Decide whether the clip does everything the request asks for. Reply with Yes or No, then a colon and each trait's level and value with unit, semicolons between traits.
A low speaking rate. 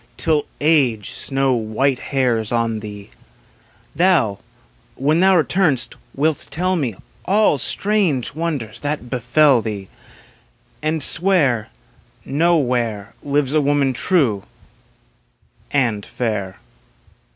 Yes: slow, 100 wpm